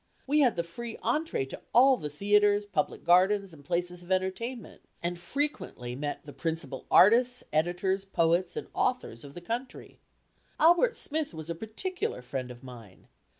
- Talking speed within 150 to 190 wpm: Yes, average, 160 wpm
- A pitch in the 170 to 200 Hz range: Yes, medium, 185 Hz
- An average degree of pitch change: No, wide, 6.9 semitones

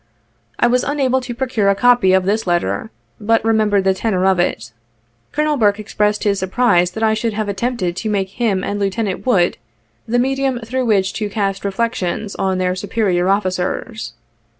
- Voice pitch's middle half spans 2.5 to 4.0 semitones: Yes, average, 3.6 semitones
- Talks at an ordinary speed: Yes, average, 175 wpm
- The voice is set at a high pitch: Yes, high, 210 Hz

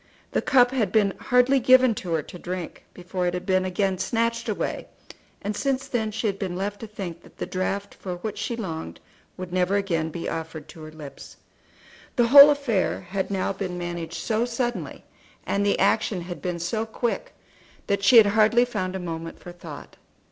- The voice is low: No, high, 195 Hz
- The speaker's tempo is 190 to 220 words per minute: Yes, average, 195 wpm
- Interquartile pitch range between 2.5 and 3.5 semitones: No, average, 4.3 semitones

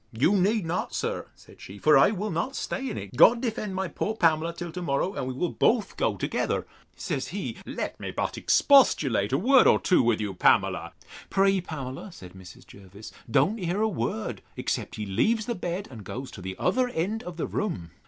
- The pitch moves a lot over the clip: Yes, wide, 8.8 semitones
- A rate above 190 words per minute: Yes, fast, 205 wpm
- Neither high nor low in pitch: Yes, medium, 175 Hz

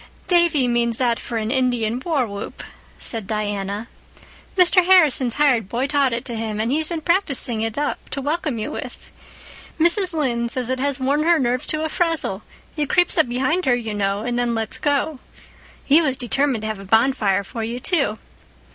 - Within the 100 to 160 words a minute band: No, average, 190 wpm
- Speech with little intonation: No, average, 5.1 semitones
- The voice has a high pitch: Yes, very high, 255 Hz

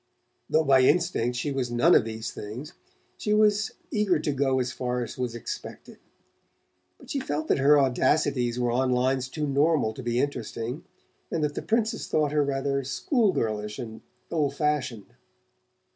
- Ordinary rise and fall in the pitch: Yes, average, 3.8 semitones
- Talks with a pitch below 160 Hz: Yes, low, 135 Hz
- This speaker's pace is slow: No, average, 170 wpm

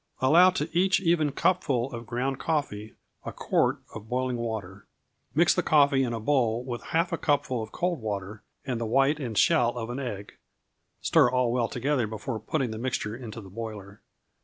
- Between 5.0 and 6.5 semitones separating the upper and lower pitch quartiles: No, average, 4.3 semitones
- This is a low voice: Yes, low, 125 Hz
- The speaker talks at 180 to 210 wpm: Yes, average, 185 wpm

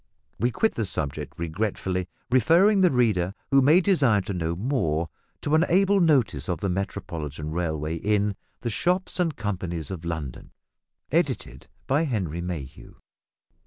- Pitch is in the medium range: No, low, 100 Hz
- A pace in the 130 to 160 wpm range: Yes, average, 145 wpm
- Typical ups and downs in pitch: No, wide, 8.7 semitones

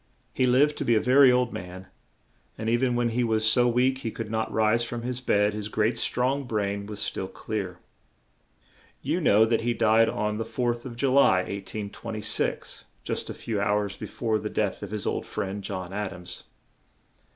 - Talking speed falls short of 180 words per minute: No, average, 200 wpm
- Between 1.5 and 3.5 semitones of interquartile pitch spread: Yes, average, 2.9 semitones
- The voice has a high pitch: No, low, 110 Hz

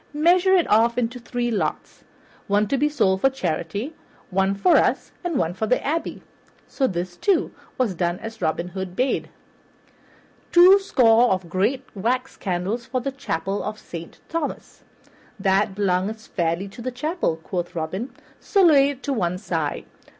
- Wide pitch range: Yes, wide, 6.5 semitones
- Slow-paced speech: No, average, 160 wpm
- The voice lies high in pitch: Yes, high, 220 Hz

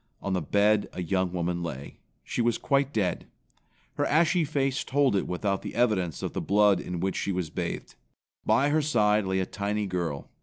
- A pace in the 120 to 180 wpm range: No, average, 195 wpm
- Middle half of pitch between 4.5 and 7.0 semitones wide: Yes, average, 5.3 semitones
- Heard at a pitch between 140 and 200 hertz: No, low, 100 Hz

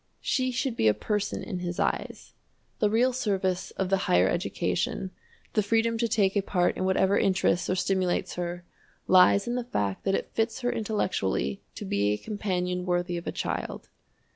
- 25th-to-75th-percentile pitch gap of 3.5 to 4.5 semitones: Yes, average, 3.8 semitones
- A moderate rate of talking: Yes, average, 185 wpm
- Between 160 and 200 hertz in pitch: Yes, high, 190 Hz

